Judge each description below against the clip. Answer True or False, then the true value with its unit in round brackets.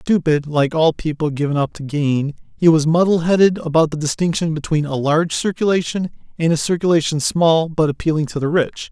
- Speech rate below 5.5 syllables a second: True (4.8 syllables/s)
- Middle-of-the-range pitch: True (160 Hz)